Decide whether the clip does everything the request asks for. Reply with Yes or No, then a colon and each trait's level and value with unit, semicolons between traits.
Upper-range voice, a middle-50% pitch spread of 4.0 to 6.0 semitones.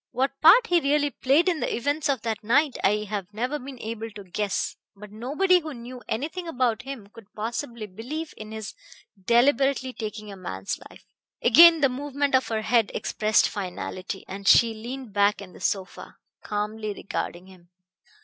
Yes: high, 235 Hz; average, 4.9 semitones